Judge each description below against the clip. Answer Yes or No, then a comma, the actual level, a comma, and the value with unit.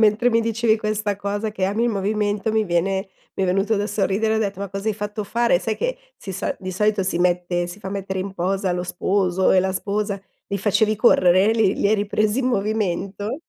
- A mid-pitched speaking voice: No, high, 200 Hz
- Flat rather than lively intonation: Yes, narrow, 2.2 semitones